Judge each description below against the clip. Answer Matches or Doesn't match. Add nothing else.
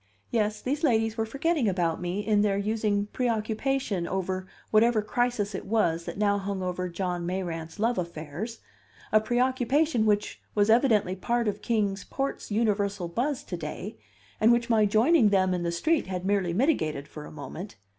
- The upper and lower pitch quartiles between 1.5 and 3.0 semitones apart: Doesn't match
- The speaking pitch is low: Doesn't match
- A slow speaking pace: Doesn't match